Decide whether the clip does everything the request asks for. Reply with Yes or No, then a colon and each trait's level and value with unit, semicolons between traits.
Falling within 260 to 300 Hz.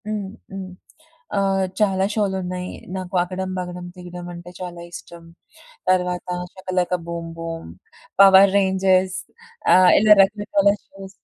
No: medium, 185 Hz